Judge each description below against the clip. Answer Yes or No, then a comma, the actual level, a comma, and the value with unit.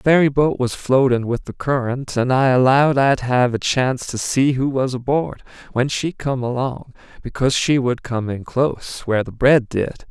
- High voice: No, low, 130 Hz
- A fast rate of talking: No, average, 195 wpm